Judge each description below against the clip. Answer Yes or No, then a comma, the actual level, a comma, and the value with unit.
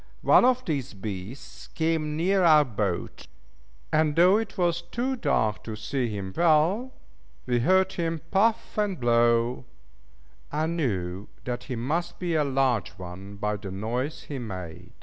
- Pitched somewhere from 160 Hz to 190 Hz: No, medium, 140 Hz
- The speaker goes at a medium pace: Yes, average, 150 wpm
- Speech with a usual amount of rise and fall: No, wide, 8.0 semitones